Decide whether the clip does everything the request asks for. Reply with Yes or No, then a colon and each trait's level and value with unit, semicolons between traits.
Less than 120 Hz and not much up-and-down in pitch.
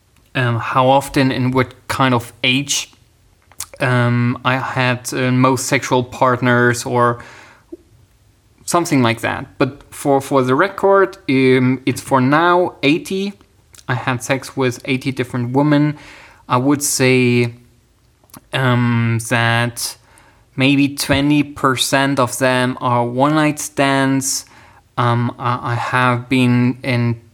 No: low, 125 Hz; narrow, 2.2 semitones